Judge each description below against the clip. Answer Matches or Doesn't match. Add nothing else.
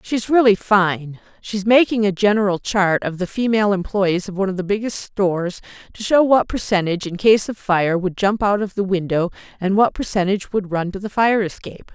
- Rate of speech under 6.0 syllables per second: Matches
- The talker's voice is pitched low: Doesn't match